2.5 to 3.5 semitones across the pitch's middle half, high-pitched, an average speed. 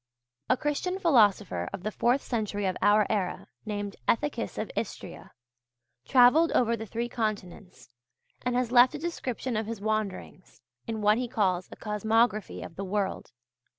Yes: average, 3.2 semitones; high, 220 Hz; average, 155 wpm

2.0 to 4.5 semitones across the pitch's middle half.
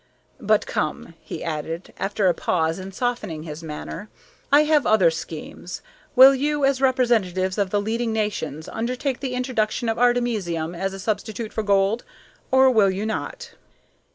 No: average, 5.1 semitones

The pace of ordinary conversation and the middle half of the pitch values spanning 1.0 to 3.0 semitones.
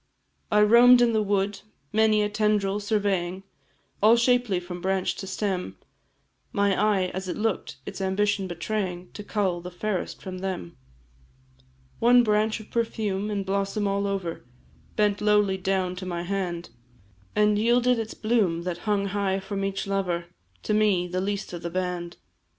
Yes: average, 160 wpm; narrow, 2.4 semitones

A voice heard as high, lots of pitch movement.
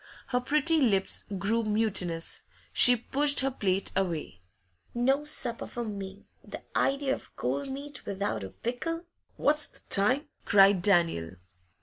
Yes: high, 225 Hz; wide, 6.0 semitones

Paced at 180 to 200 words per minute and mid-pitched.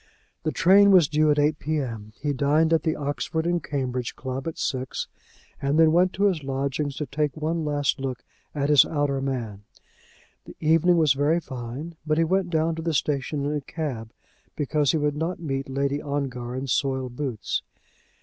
Yes: average, 190 wpm; medium, 145 Hz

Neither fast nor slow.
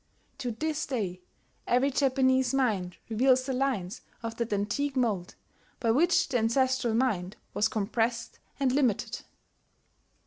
No: slow, 130 wpm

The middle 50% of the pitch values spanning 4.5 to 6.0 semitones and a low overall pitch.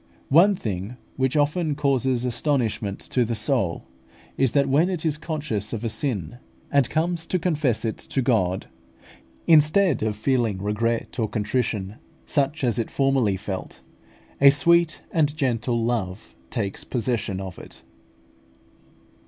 Yes: average, 5.3 semitones; low, 125 Hz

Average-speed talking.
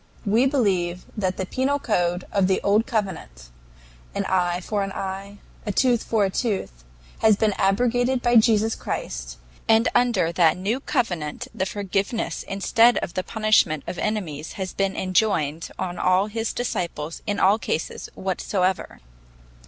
Yes: average, 160 wpm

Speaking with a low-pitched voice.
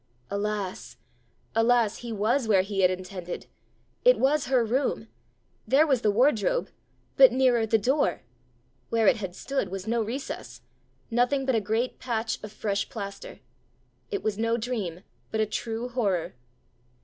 No: high, 225 Hz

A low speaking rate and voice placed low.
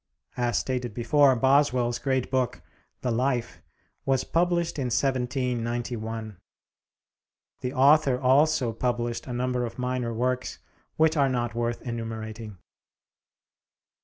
Yes: slow, 110 wpm; low, 125 Hz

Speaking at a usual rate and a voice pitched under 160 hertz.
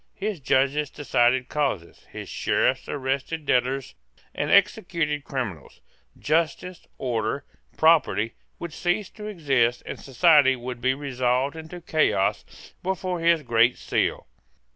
No: slow, 120 wpm; medium, 140 Hz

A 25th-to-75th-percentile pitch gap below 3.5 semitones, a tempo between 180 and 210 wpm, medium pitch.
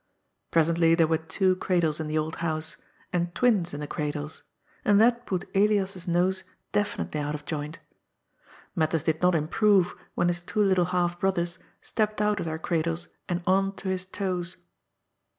No: average, 3.1 semitones; average, 170 wpm; medium, 175 Hz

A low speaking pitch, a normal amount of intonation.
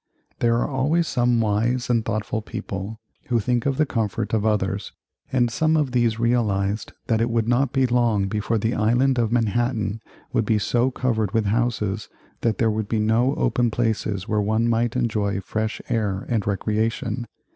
No: low, 115 Hz; narrow, 2.3 semitones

